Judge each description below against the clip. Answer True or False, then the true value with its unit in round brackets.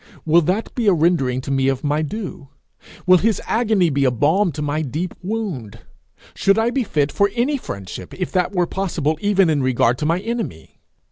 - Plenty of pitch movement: True (6.3 semitones)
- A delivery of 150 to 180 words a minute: False (200 wpm)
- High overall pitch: False (170 Hz)